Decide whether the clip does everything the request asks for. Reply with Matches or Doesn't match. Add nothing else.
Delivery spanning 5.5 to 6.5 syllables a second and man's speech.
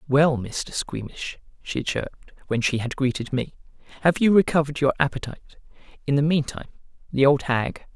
Matches